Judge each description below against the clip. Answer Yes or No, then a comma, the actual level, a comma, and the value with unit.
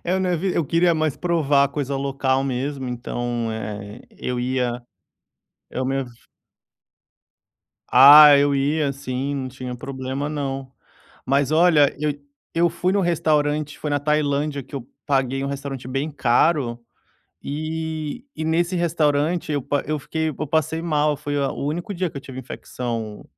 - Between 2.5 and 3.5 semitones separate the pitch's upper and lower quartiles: Yes, average, 2.8 semitones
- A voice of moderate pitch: Yes, medium, 145 Hz